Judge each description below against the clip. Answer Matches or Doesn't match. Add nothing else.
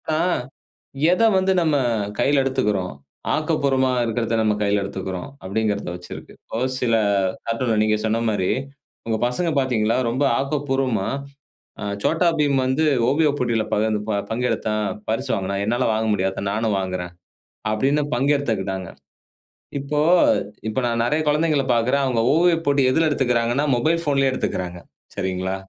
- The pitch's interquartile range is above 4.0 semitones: Matches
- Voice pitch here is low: Matches